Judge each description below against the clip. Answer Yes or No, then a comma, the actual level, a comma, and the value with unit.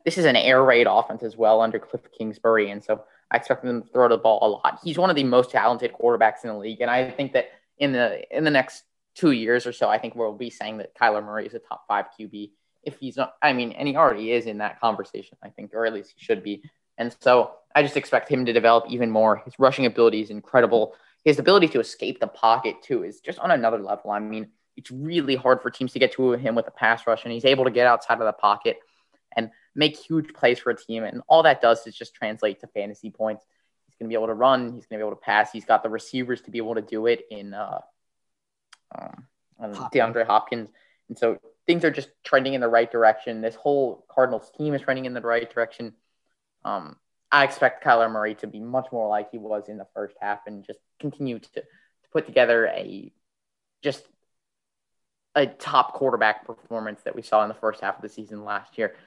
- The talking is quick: Yes, fast, 240 wpm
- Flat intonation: No, average, 3.2 semitones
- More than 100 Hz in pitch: Yes, low, 115 Hz